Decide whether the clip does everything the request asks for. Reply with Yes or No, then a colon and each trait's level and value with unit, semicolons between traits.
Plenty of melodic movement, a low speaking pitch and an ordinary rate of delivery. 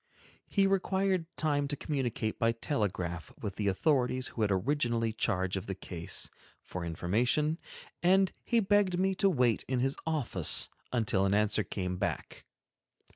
Yes: wide, 8.4 semitones; low, 125 Hz; average, 150 wpm